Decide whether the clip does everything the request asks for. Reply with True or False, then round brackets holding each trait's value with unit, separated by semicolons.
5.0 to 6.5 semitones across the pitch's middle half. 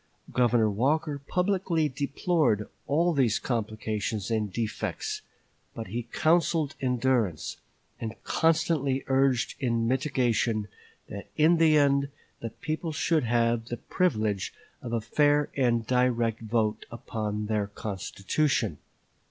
True (5.3 semitones)